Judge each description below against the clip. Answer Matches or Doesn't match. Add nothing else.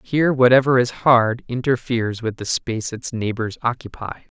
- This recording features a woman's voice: Doesn't match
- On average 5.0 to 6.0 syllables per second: Matches